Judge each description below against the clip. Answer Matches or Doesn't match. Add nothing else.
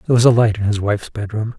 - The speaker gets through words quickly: Matches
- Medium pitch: Doesn't match